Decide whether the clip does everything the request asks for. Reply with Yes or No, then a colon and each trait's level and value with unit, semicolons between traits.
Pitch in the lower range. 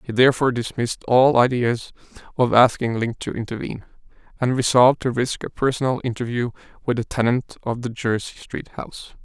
Yes: low, 120 Hz